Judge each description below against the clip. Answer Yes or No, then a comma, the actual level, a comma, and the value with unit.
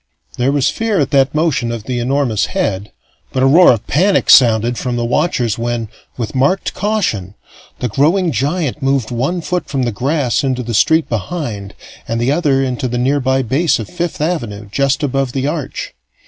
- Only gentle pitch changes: No, average, 4.3 semitones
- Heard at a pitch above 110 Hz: Yes, low, 135 Hz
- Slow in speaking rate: No, average, 185 wpm